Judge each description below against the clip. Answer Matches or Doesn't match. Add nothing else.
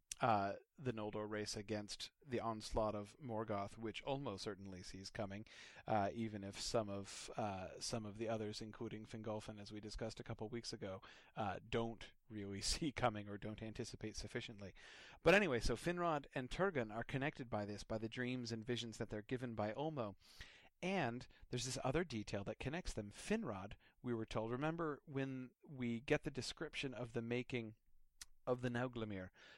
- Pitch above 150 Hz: Doesn't match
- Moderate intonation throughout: Matches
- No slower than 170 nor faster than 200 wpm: Matches